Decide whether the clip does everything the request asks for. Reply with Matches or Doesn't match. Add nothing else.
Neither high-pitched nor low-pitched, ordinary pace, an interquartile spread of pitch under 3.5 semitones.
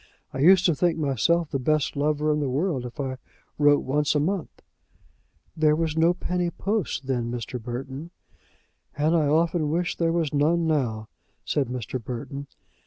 Doesn't match